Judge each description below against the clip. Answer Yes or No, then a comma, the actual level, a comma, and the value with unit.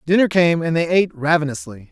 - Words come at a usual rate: Yes, average, 190 wpm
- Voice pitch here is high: No, medium, 165 Hz